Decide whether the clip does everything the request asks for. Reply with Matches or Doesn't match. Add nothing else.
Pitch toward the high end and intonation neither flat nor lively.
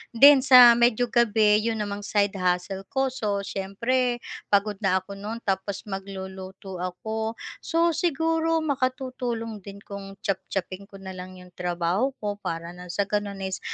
Matches